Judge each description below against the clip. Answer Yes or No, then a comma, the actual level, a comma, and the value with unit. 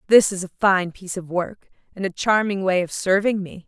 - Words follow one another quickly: Yes, fast, 230 wpm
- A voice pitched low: No, high, 190 Hz